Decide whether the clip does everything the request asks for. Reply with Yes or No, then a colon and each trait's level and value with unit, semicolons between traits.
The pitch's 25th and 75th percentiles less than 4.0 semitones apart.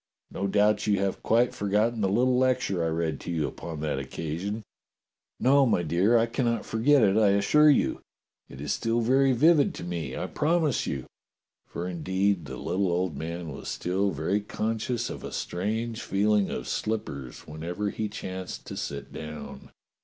No: average, 5.2 semitones